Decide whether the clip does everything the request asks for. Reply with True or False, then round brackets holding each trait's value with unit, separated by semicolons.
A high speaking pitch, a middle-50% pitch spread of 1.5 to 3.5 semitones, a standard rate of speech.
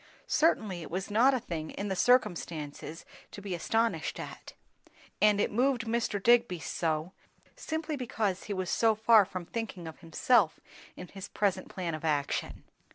False (200 Hz; 4.9 semitones; 160 wpm)